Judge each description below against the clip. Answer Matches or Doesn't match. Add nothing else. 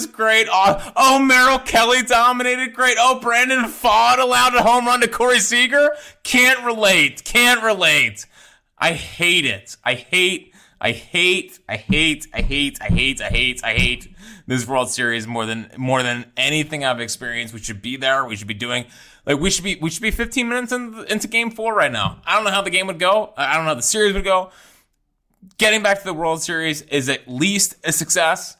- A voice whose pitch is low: Doesn't match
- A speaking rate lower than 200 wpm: Doesn't match